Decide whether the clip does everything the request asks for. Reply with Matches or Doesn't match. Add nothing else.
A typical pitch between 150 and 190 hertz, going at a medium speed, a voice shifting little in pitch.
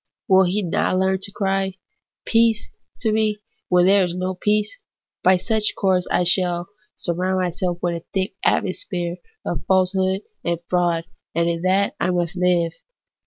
Matches